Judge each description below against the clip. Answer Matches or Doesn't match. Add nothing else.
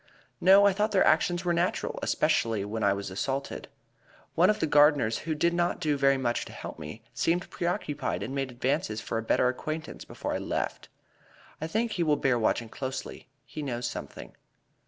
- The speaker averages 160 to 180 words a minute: Doesn't match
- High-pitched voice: Doesn't match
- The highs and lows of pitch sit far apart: Matches